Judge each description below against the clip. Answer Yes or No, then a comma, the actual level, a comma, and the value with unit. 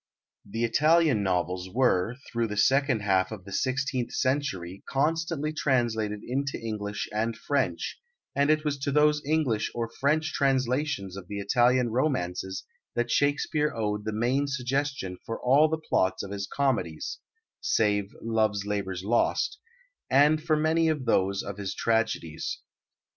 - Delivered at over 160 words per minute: No, average, 145 wpm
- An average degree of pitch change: No, wide, 5.8 semitones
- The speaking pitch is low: Yes, low, 120 Hz